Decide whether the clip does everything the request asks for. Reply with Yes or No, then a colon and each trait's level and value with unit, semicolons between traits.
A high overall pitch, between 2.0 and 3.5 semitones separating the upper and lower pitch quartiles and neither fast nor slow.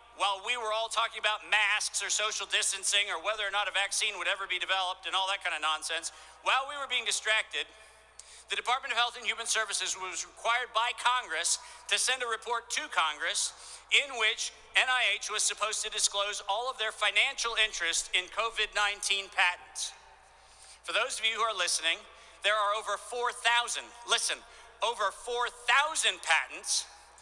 Yes: high, 215 Hz; average, 2.8 semitones; average, 175 wpm